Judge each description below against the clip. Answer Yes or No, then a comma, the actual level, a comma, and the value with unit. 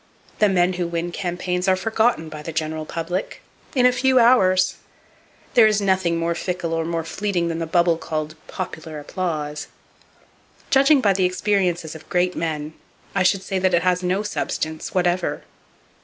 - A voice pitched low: No, medium, 180 Hz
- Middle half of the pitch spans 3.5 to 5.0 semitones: No, average, 2.7 semitones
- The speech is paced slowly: No, average, 170 wpm